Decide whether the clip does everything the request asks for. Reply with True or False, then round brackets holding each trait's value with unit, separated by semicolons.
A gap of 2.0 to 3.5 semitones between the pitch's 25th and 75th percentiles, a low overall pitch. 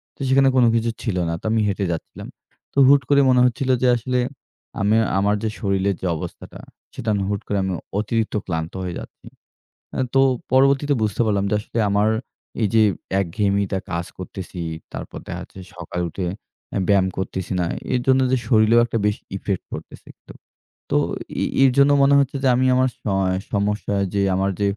False (4.6 semitones; 105 Hz)